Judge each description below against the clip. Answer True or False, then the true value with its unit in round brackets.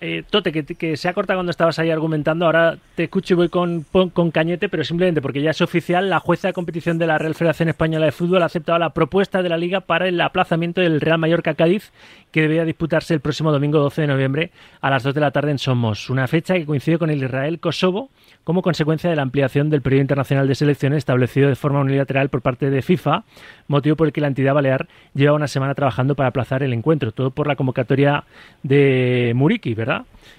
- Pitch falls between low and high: True (155 Hz)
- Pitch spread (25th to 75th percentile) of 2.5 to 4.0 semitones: True (3.4 semitones)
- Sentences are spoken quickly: True (225 wpm)